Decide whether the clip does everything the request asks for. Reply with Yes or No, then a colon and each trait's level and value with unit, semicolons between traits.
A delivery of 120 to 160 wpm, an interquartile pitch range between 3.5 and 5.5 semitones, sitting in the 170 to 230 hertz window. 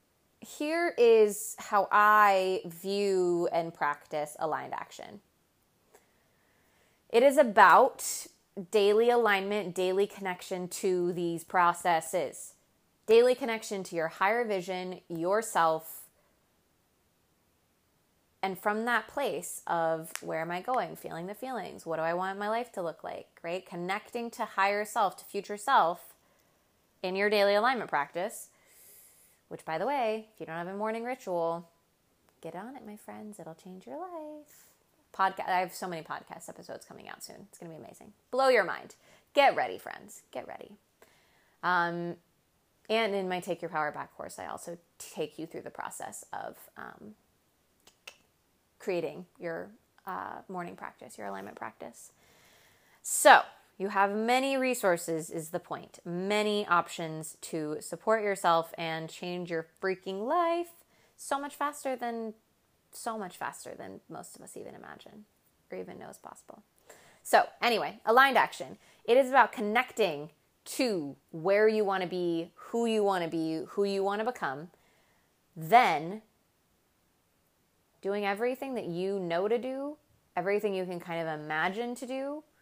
Yes: average, 145 wpm; average, 4.7 semitones; high, 190 Hz